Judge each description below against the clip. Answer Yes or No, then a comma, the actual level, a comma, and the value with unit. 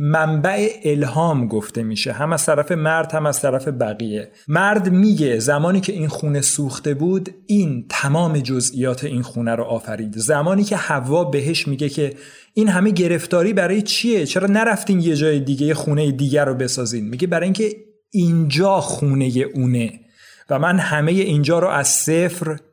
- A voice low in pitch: No, medium, 155 Hz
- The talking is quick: Yes, fast, 160 wpm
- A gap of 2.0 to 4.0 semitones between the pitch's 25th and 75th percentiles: No, average, 4.6 semitones